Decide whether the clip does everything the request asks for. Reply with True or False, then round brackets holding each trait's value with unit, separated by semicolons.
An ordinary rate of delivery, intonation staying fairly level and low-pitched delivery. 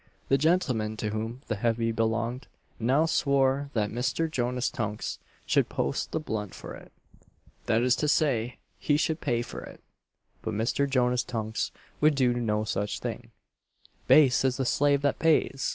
False (165 wpm; 3.8 semitones; 125 Hz)